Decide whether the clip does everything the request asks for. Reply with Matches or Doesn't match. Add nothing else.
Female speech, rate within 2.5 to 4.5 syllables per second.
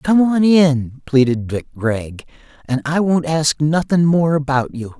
Doesn't match